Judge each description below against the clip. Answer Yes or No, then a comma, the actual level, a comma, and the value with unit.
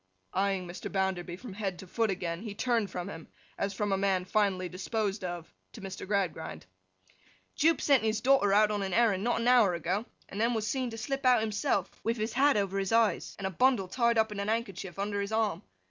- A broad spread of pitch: No, average, 3.0 semitones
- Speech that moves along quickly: Yes, fast, 225 wpm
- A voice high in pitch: Yes, high, 205 Hz